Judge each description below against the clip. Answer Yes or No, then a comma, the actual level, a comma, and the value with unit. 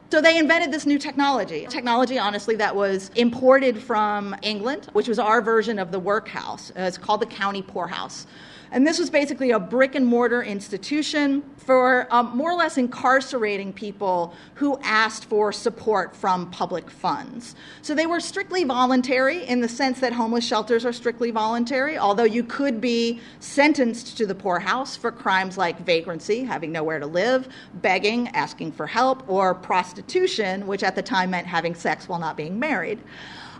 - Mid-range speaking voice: No, high, 235 Hz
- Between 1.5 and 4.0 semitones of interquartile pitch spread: No, average, 4.6 semitones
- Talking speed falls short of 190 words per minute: Yes, average, 170 wpm